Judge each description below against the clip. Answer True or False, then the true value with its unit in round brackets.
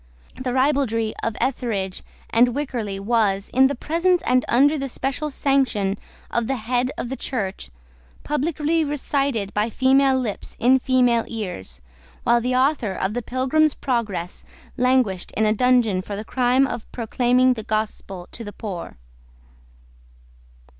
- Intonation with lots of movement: False (3.7 semitones)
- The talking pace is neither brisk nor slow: True (145 wpm)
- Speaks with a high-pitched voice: True (245 Hz)